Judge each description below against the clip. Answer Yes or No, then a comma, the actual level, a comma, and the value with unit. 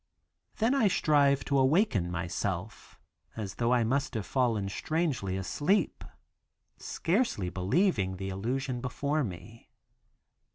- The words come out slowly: Yes, slow, 115 wpm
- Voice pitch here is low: Yes, low, 120 Hz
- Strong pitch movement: Yes, wide, 7.4 semitones